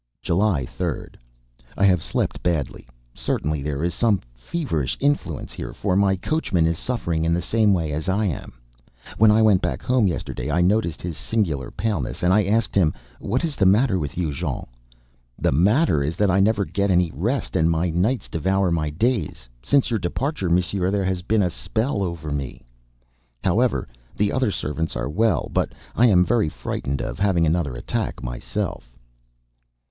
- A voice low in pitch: Yes, very low, 90 Hz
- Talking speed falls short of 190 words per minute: Yes, average, 180 wpm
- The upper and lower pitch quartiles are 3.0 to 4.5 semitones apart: No, average, 5.0 semitones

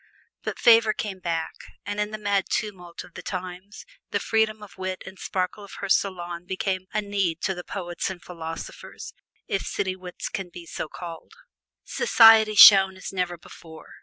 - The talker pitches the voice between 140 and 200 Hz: Yes, high, 190 Hz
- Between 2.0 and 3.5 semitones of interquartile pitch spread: Yes, narrow, 2.5 semitones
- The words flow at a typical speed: Yes, average, 175 wpm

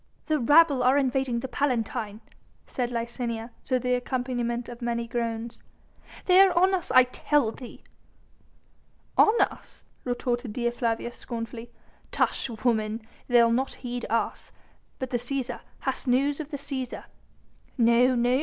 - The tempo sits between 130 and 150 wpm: Yes, average, 140 wpm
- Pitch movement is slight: Yes, narrow, 2.1 semitones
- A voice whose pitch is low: No, high, 245 Hz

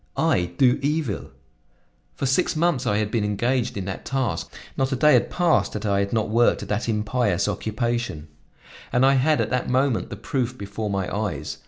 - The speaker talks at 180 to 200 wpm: Yes, average, 195 wpm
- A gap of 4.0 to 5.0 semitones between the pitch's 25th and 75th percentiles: Yes, average, 4.3 semitones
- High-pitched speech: No, low, 120 Hz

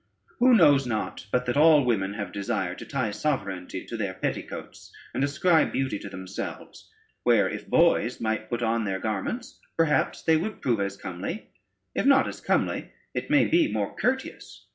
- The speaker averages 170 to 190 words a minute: Yes, average, 175 wpm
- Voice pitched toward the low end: Yes, low, 120 Hz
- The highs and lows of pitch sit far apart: Yes, wide, 7.6 semitones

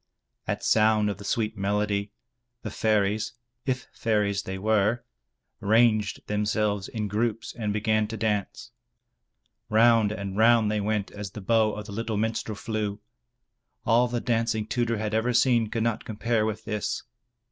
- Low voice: Yes, low, 110 Hz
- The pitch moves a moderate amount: No, narrow, 1.6 semitones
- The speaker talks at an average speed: Yes, average, 155 wpm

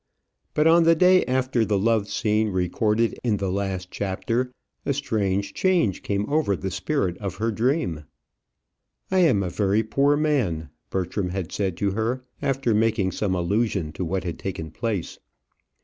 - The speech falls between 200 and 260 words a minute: No, average, 165 wpm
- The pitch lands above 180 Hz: No, low, 105 Hz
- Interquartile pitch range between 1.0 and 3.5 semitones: No, average, 5.1 semitones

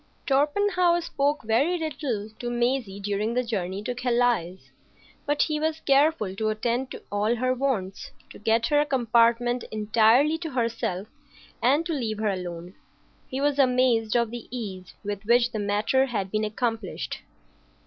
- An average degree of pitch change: Yes, average, 4.2 semitones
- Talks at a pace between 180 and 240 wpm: No, average, 160 wpm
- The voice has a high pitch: Yes, high, 240 Hz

